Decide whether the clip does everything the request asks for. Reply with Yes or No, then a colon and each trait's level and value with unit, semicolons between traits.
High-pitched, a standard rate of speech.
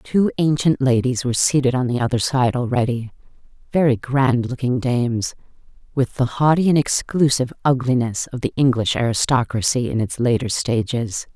No: low, 125 Hz; average, 145 wpm